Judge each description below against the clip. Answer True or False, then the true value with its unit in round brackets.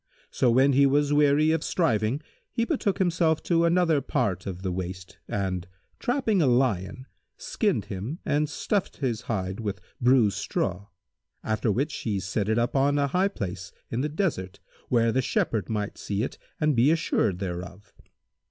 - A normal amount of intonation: False (7.2 semitones)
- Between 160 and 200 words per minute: True (170 wpm)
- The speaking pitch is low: True (125 Hz)